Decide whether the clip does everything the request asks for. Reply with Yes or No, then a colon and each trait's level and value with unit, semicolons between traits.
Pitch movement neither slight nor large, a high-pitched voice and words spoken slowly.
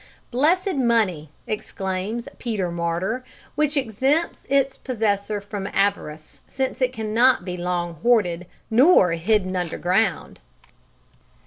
No: wide, 5.9 semitones; high, 210 Hz; slow, 105 wpm